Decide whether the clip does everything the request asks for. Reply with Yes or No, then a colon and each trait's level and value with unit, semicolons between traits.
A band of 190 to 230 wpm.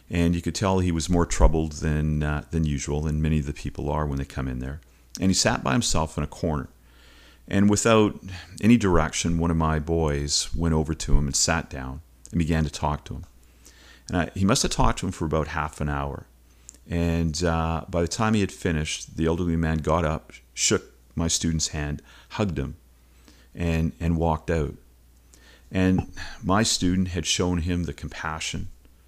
Yes: average, 200 wpm